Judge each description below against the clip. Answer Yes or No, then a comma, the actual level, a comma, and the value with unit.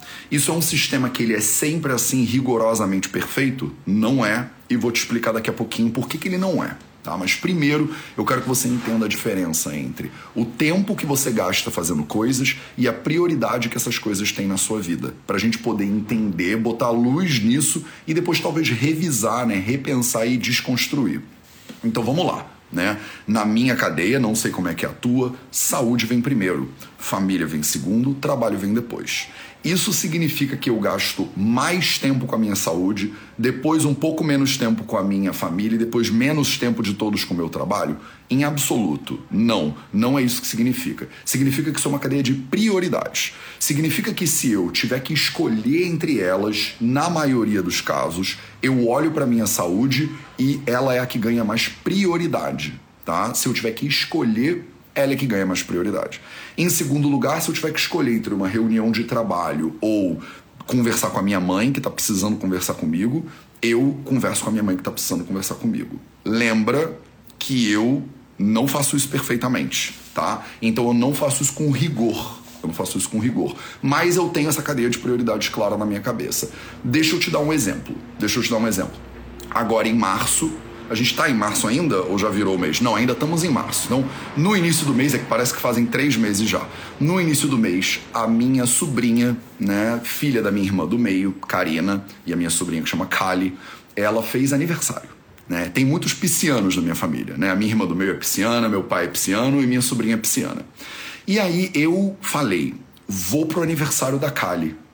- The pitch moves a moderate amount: Yes, average, 5.0 semitones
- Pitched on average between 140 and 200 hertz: No, low, 125 Hz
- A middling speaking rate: No, fast, 200 wpm